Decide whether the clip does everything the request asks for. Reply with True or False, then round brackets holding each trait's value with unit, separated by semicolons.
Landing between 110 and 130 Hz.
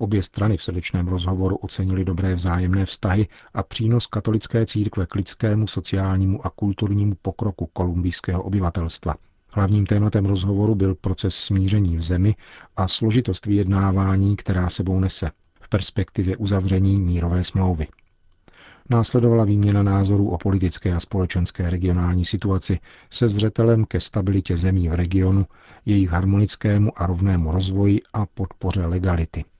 False (95 Hz)